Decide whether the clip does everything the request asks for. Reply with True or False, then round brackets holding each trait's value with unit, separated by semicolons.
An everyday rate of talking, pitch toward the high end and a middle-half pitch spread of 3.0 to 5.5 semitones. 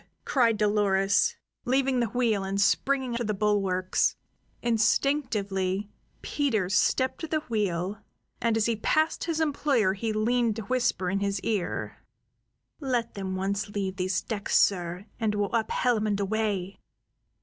True (145 wpm; 215 Hz; 3.7 semitones)